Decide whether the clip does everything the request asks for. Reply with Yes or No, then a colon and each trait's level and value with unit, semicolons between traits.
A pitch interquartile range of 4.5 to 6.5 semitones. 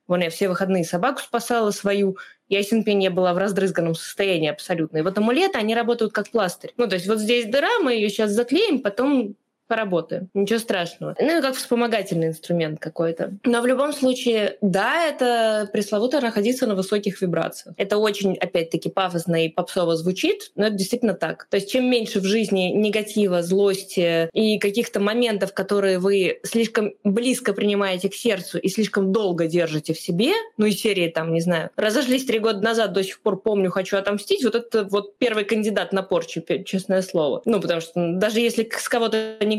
No: average, 3.4 semitones